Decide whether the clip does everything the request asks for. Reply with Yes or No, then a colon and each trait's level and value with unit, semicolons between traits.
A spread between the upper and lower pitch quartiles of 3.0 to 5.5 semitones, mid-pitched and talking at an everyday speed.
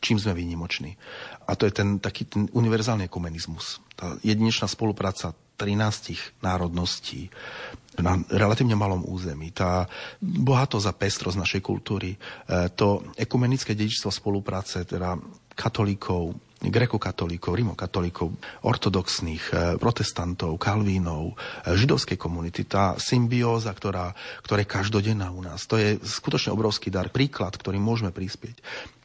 No: average, 3.5 semitones; low, 100 Hz; average, 120 wpm